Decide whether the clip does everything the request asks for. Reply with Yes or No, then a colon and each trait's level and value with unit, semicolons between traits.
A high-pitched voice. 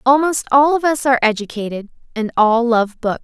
Yes: very high, 250 Hz